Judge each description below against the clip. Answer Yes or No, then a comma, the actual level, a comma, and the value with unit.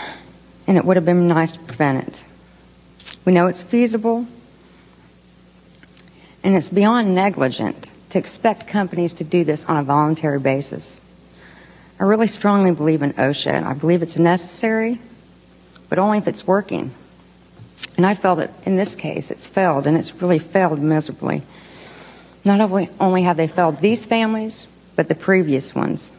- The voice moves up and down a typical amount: Yes, average, 4.5 semitones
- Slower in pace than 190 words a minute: Yes, average, 155 wpm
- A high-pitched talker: No, medium, 180 Hz